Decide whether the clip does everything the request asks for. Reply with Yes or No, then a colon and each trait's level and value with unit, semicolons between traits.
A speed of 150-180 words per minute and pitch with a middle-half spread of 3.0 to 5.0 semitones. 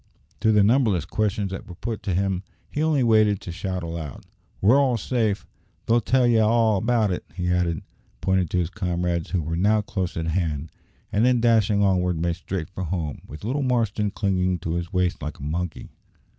No: average, 200 wpm; average, 4.1 semitones